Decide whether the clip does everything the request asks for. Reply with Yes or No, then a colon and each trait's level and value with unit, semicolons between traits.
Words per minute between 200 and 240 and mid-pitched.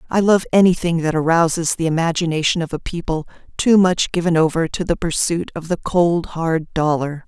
No: average, 180 wpm; medium, 165 Hz